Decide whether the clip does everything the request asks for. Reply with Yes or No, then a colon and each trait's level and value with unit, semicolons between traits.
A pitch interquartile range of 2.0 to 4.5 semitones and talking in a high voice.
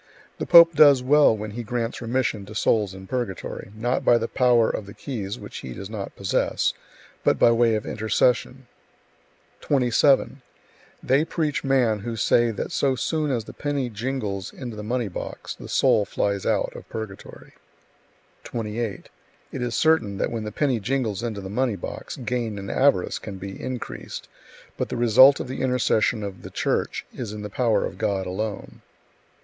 No: average, 3.6 semitones; low, 115 Hz